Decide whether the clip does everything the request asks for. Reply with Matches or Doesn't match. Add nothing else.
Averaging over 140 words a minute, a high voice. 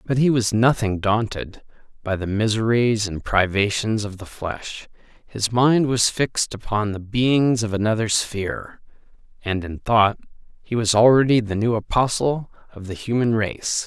Doesn't match